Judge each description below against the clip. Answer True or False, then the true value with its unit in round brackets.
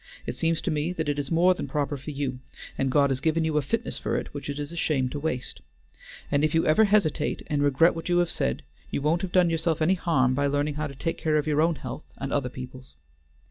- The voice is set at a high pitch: False (150 Hz)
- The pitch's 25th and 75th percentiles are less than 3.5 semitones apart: True (2.8 semitones)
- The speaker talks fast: True (260 wpm)